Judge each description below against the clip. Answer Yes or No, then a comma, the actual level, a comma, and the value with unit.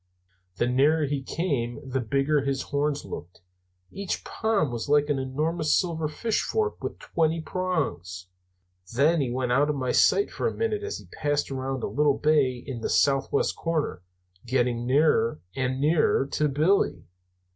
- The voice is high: No, medium, 145 Hz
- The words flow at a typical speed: Yes, average, 165 wpm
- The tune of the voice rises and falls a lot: No, average, 3.5 semitones